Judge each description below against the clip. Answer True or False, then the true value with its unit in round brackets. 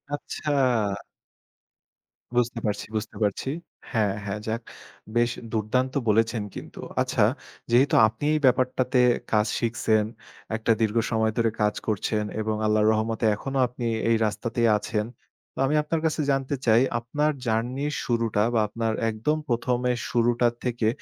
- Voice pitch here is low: True (115 Hz)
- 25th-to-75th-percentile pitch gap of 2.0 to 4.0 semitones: True (2.4 semitones)